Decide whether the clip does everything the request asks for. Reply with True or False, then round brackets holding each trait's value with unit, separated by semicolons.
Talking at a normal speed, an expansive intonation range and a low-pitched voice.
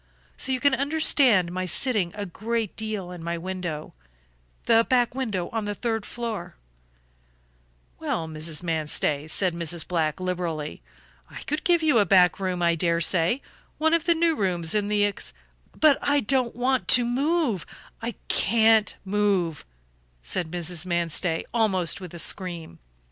False (160 wpm; 5.8 semitones; 190 Hz)